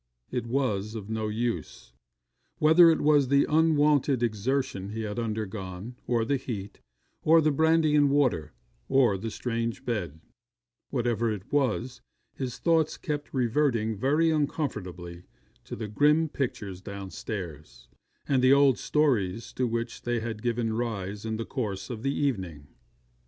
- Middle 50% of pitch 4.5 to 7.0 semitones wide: Yes, average, 5.0 semitones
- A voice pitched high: No, low, 120 Hz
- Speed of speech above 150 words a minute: No, average, 145 wpm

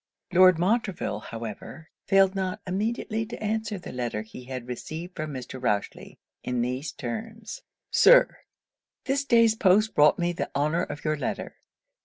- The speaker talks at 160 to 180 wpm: No, average, 150 wpm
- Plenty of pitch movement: Yes, wide, 8.9 semitones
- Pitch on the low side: No, medium, 175 Hz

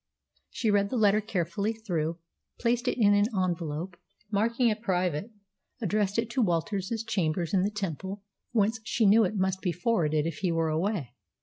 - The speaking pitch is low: No, high, 200 Hz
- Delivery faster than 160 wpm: Yes, average, 180 wpm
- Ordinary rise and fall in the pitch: Yes, average, 4.0 semitones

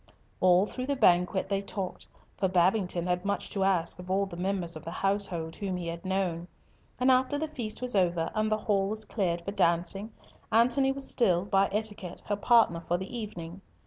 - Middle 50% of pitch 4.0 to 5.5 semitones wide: No, average, 3.4 semitones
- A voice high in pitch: Yes, high, 195 Hz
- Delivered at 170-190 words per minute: No, average, 200 wpm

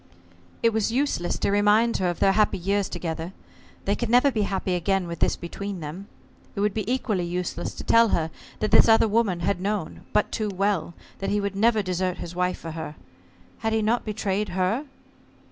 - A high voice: Yes, high, 200 Hz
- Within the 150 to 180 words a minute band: No, average, 200 wpm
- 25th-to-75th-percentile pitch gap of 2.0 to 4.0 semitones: Yes, average, 3.3 semitones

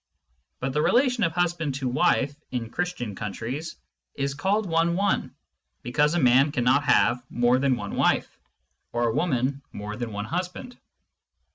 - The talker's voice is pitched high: No, medium, 140 Hz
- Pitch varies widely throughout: Yes, wide, 5.8 semitones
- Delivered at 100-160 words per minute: Yes, average, 155 wpm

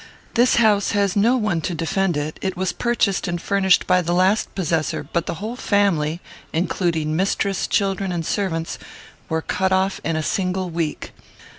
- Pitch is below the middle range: No, medium, 185 Hz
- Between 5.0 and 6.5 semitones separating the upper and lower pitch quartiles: No, average, 3.2 semitones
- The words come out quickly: No, average, 170 wpm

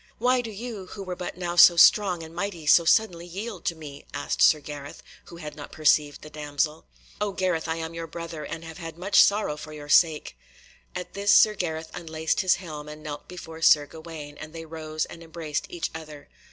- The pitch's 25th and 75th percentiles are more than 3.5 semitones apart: No, average, 2.8 semitones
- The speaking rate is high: Yes, fast, 210 wpm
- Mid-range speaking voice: Yes, medium, 165 Hz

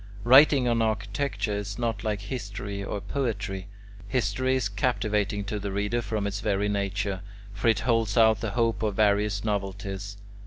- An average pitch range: No, narrow, 2.3 semitones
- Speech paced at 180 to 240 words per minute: No, average, 160 wpm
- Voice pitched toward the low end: Yes, low, 105 Hz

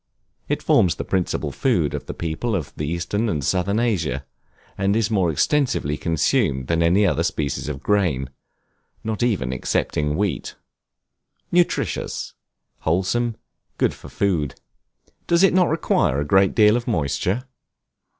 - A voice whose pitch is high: No, very low, 95 Hz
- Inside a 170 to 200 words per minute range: No, average, 140 wpm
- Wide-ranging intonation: Yes, wide, 6.5 semitones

